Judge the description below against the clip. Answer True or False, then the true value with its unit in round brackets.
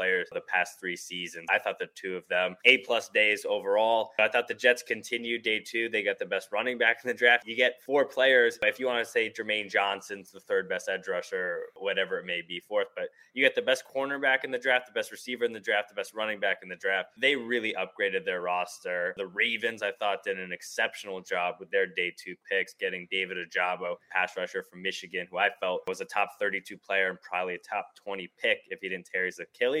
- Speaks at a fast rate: True (240 wpm)